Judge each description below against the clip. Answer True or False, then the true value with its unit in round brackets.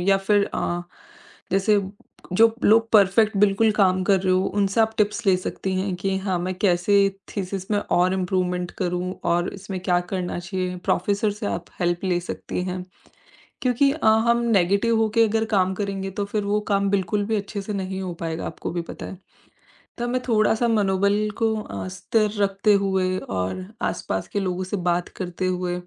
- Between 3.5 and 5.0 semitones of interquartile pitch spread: False (2.4 semitones)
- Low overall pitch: False (195 Hz)